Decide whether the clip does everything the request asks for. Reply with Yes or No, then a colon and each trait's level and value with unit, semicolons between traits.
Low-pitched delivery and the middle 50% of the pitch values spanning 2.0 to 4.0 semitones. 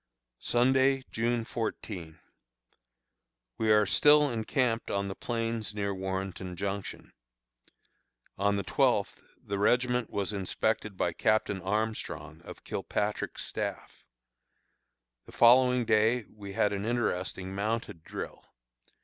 Yes: low, 105 Hz; average, 3.1 semitones